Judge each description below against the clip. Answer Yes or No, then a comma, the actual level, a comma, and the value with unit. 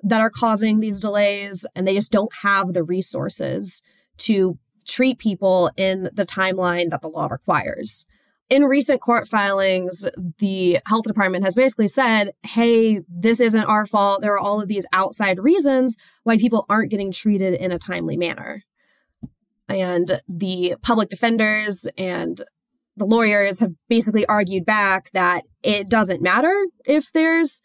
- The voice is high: Yes, high, 205 Hz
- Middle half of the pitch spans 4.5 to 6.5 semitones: No, average, 3.3 semitones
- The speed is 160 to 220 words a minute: No, average, 150 wpm